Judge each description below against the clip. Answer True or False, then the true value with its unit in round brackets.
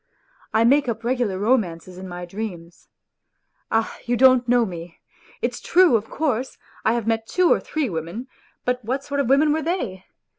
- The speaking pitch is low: False (235 Hz)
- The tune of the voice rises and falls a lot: True (5.7 semitones)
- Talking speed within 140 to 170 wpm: False (185 wpm)